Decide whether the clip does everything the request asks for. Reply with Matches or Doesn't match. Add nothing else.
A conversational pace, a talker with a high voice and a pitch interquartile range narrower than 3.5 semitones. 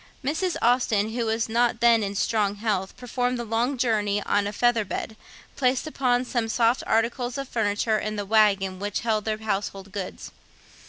Matches